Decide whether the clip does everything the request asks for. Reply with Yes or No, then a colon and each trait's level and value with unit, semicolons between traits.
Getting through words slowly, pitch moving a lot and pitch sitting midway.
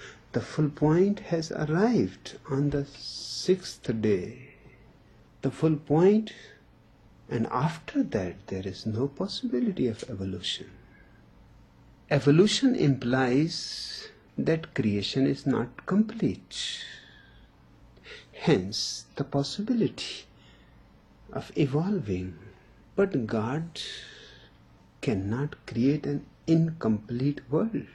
Yes: slow, 85 wpm; wide, 7.2 semitones; medium, 145 Hz